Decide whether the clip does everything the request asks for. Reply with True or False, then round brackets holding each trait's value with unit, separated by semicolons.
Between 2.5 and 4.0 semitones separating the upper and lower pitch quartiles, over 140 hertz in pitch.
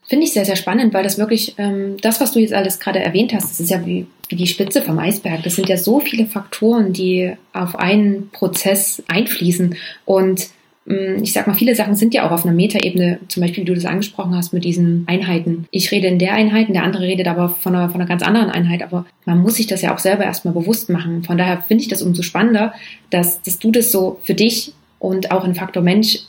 True (2.8 semitones; 190 Hz)